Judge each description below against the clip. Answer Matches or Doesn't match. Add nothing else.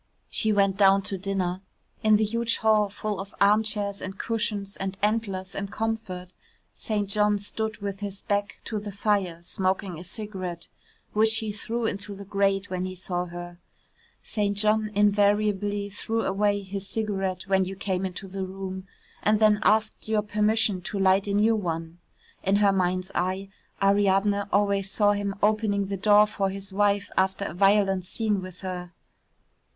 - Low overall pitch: Doesn't match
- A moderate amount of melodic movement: Doesn't match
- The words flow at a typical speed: Matches